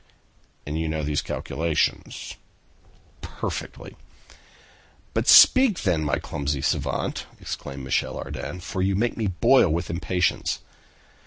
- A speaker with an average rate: No, slow, 115 wpm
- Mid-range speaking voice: No, very low, 85 Hz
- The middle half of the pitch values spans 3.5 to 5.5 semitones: Yes, average, 4.1 semitones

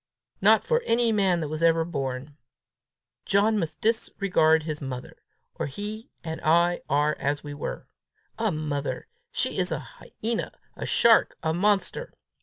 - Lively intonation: Yes, wide, 6.0 semitones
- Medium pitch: Yes, medium, 165 Hz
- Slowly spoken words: No, average, 150 wpm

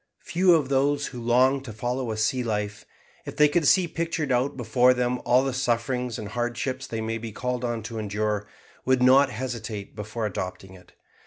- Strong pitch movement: No, average, 3.2 semitones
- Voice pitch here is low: Yes, low, 120 Hz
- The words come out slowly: No, average, 190 wpm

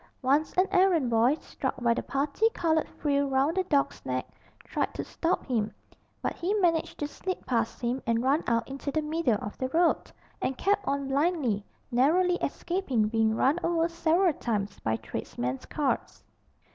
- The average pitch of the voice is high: Yes, very high, 280 Hz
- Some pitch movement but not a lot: No, wide, 6.0 semitones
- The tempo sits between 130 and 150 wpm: No, average, 170 wpm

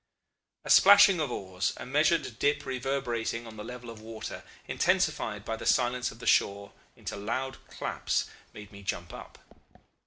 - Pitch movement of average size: Yes, average, 4.5 semitones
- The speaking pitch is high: No, low, 120 Hz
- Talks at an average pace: Yes, average, 160 wpm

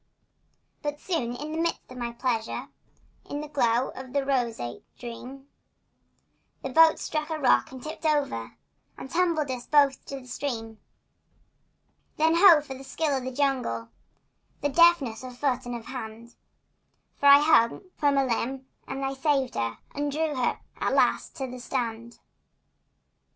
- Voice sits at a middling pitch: No, very high, 270 Hz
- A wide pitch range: No, average, 3.3 semitones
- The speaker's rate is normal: Yes, average, 160 wpm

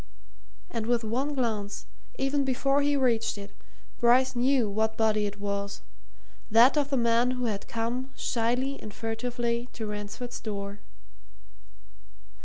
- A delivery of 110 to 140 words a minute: Yes, slow, 135 wpm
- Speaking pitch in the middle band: No, high, 235 Hz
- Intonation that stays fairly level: No, average, 3.1 semitones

